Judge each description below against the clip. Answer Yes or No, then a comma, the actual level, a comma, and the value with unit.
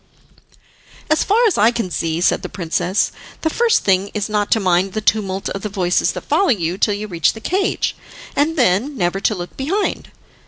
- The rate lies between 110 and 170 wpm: No, average, 200 wpm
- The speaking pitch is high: Yes, high, 205 Hz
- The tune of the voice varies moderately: No, wide, 7.1 semitones